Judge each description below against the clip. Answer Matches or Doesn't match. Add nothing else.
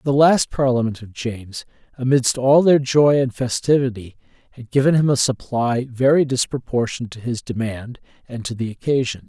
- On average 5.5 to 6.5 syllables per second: Doesn't match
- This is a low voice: Matches